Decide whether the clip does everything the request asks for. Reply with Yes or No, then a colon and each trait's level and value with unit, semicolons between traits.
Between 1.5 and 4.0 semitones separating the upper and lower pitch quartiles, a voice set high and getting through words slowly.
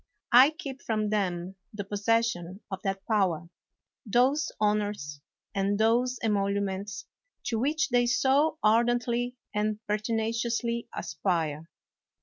Yes: average, 3.4 semitones; high, 215 Hz; slow, 110 wpm